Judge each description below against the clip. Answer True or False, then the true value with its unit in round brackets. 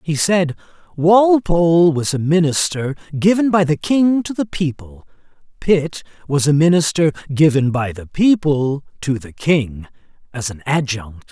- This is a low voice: False (150 Hz)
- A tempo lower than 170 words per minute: True (140 wpm)